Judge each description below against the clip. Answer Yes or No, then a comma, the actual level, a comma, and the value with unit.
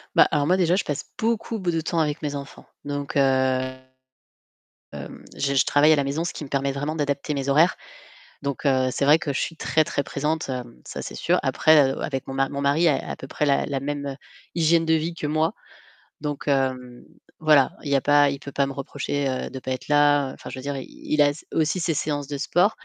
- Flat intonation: Yes, narrow, 2.3 semitones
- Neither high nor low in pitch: Yes, medium, 145 Hz